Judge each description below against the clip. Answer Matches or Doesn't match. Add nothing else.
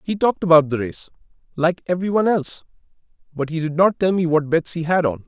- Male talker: Matches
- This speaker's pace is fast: Matches